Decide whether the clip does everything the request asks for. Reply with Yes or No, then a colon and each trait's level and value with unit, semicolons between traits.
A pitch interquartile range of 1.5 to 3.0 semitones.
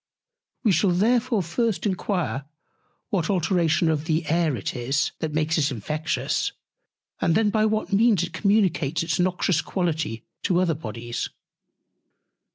No: average, 4.4 semitones